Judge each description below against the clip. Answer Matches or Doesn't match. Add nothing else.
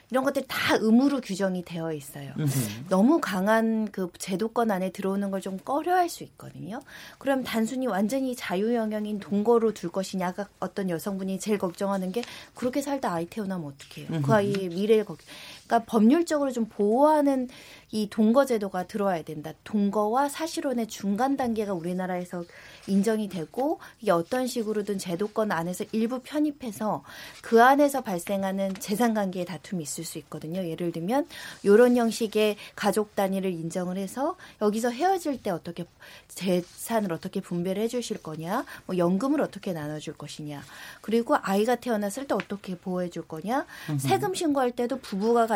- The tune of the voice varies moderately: Matches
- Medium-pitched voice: Doesn't match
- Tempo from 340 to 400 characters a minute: Matches